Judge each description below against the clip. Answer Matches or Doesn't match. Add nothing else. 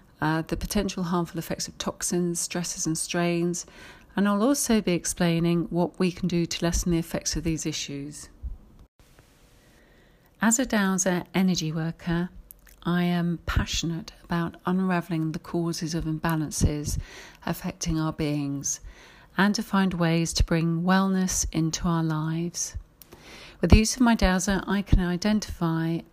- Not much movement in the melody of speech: Matches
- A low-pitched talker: Doesn't match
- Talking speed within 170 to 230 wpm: Doesn't match